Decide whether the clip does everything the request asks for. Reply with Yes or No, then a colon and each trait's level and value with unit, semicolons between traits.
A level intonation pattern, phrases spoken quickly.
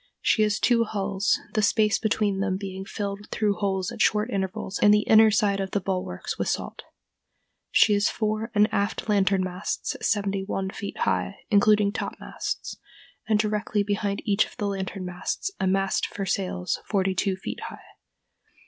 No: narrow, 1.6 semitones; average, 170 wpm